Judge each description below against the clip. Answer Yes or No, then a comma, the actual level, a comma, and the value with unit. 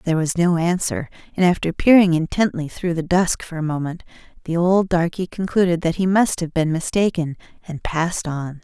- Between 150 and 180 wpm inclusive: No, average, 190 wpm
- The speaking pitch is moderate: Yes, medium, 170 Hz